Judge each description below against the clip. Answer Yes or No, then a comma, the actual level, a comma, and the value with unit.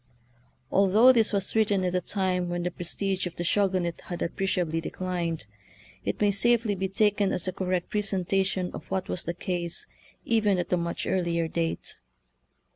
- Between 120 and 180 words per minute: Yes, average, 175 wpm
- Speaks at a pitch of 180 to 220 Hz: Yes, medium, 185 Hz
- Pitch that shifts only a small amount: Yes, narrow, 2.3 semitones